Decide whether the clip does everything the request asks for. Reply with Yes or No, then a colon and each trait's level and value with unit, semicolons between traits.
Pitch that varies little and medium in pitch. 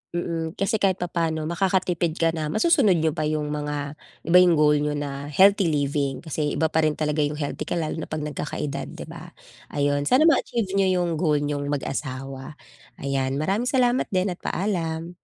No: average, 3.5 semitones; medium, 155 Hz